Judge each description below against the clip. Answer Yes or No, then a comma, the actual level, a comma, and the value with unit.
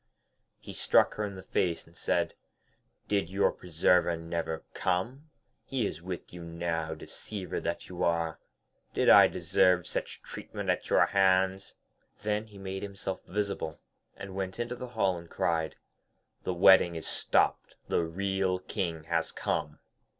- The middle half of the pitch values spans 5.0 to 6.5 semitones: No, average, 2.8 semitones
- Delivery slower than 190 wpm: Yes, average, 150 wpm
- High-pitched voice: No, very low, 95 Hz